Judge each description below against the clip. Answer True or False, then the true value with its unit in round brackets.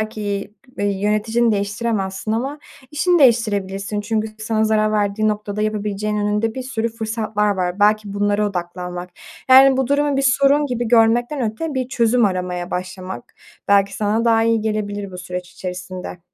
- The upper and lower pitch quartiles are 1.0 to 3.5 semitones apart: True (2.6 semitones)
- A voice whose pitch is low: False (215 Hz)